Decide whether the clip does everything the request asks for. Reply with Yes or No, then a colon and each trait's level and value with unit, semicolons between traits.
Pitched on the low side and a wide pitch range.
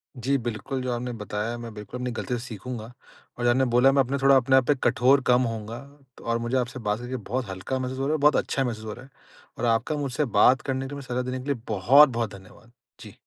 No: low, 125 Hz; narrow, 2.4 semitones